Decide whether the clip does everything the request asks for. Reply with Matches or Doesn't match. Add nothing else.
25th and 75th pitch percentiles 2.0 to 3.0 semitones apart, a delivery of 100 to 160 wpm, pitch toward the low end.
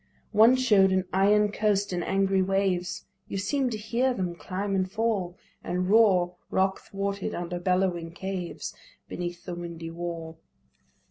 Doesn't match